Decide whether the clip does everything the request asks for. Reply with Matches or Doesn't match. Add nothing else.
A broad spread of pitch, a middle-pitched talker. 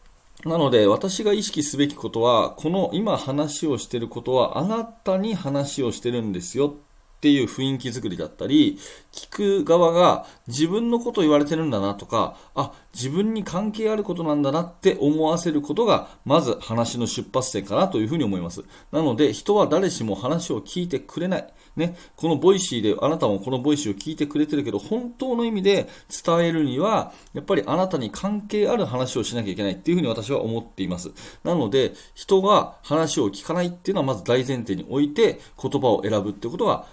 Matches